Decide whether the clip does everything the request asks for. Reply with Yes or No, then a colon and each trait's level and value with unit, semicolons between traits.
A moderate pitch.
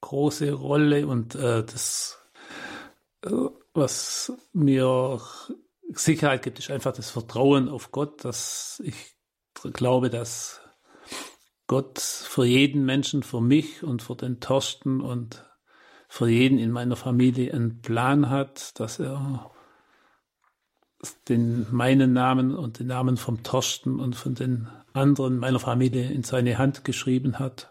No: low, 130 Hz